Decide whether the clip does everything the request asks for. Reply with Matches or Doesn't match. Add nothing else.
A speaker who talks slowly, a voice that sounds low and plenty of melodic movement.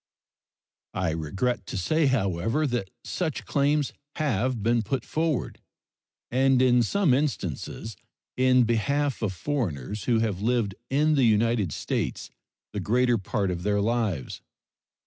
Doesn't match